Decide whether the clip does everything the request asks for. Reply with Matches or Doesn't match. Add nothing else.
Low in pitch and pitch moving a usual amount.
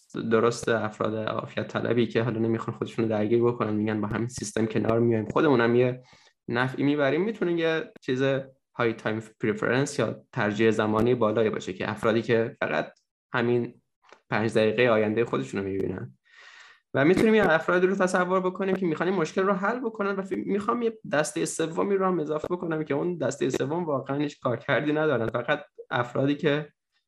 Doesn't match